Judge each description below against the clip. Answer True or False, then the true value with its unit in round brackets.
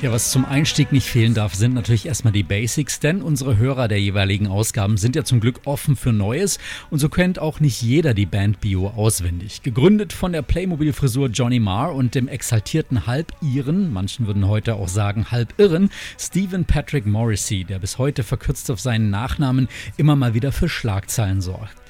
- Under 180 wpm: False (190 wpm)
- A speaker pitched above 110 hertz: True (125 Hz)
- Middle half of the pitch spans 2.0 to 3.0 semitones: False (5.4 semitones)